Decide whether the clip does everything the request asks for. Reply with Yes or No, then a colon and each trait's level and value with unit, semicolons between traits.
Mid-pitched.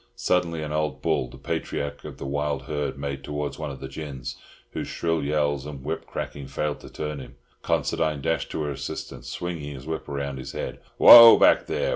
No: very low, 75 Hz